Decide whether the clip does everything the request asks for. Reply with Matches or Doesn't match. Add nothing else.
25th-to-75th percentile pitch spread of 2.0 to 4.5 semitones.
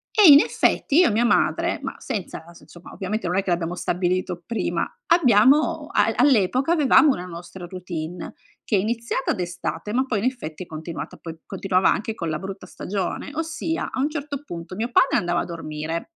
Doesn't match